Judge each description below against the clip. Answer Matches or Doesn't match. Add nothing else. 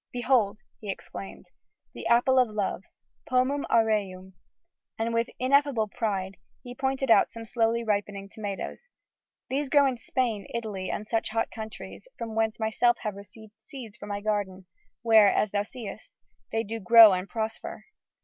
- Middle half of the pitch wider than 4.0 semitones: Doesn't match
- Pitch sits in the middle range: Doesn't match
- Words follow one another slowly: Doesn't match